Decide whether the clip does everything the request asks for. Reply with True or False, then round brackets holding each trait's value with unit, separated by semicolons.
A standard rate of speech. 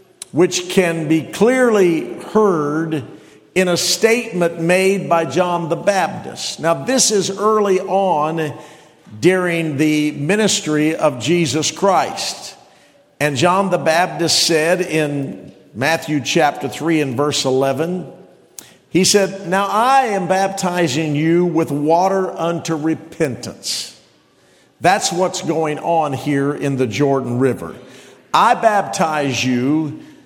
False (115 wpm)